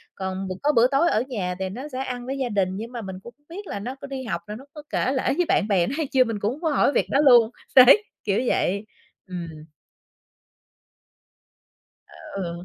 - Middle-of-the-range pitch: No, high, 240 Hz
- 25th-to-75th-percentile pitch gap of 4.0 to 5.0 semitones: No, wide, 5.6 semitones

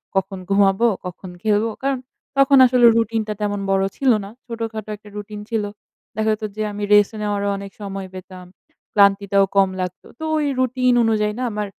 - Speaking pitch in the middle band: No, high, 210 Hz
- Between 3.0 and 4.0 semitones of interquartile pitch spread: No, narrow, 2.5 semitones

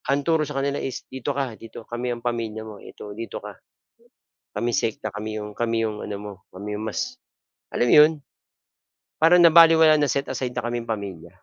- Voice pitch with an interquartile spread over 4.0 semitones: Yes, average, 4.5 semitones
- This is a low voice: Yes, low, 120 Hz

